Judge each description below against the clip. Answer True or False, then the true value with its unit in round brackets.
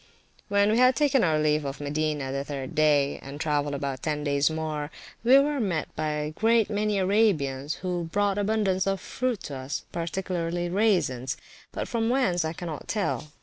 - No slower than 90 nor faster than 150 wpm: False (185 wpm)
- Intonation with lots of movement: True (5.7 semitones)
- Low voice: False (165 Hz)